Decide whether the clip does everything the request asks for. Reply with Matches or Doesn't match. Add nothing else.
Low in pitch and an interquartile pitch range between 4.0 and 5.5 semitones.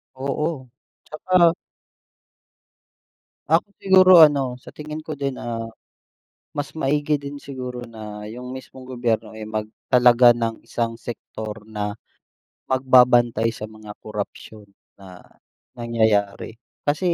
Matches